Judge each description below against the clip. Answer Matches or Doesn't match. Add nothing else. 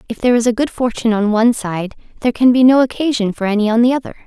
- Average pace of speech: Doesn't match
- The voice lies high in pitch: Matches